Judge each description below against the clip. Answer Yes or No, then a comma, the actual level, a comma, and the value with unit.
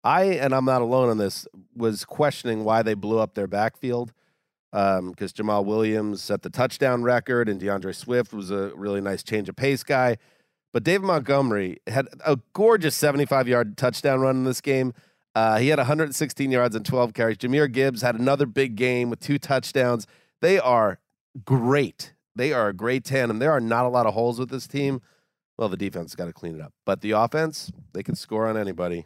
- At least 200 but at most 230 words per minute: Yes, fast, 205 wpm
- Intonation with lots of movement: No, average, 4.2 semitones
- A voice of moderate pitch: No, low, 120 Hz